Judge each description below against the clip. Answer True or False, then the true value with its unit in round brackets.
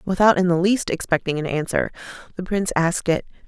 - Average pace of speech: True (190 wpm)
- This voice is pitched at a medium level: True (180 Hz)